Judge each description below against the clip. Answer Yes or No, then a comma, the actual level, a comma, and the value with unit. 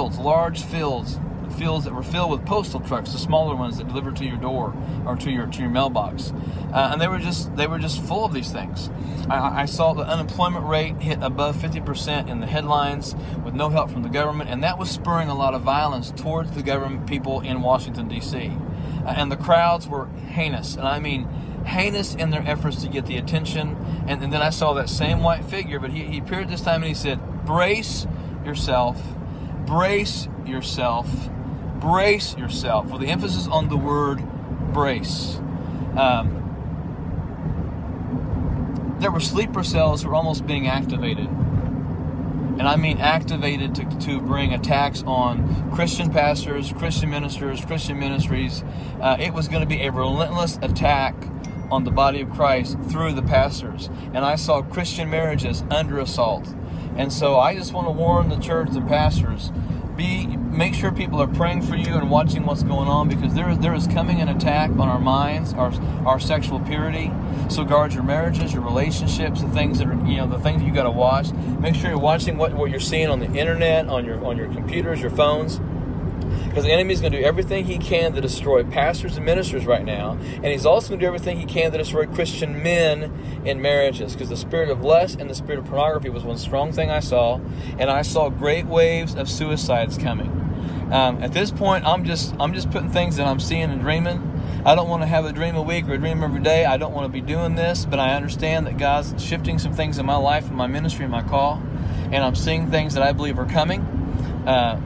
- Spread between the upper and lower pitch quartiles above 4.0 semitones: No, average, 3.0 semitones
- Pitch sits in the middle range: Yes, medium, 145 Hz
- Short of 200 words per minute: No, fast, 205 wpm